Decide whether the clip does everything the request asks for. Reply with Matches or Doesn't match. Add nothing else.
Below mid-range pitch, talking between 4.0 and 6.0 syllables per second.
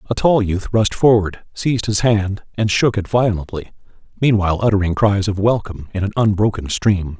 Matches